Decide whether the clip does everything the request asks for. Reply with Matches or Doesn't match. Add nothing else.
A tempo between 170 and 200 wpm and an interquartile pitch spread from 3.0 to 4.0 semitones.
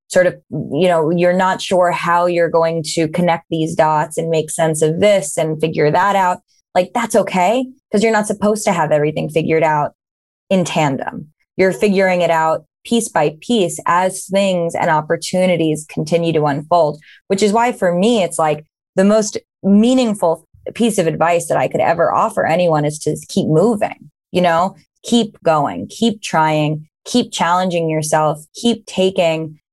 Matches